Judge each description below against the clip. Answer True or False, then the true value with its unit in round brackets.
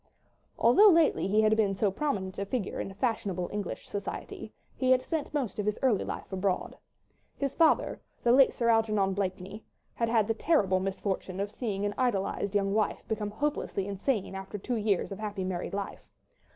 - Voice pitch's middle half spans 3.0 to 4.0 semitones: True (3.4 semitones)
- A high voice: True (205 Hz)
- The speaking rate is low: False (180 wpm)